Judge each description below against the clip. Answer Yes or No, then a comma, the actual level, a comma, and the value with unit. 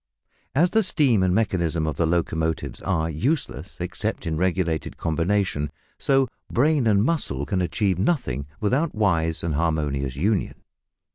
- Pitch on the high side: No, very low, 90 Hz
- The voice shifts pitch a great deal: Yes, wide, 5.9 semitones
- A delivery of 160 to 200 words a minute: No, average, 140 wpm